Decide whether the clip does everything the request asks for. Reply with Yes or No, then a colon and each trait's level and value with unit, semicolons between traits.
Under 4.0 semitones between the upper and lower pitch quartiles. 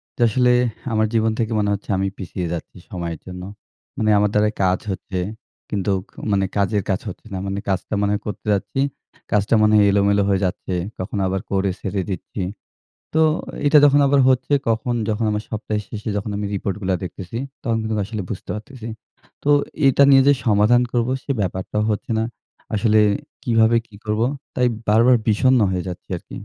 Yes: average, 2.8 semitones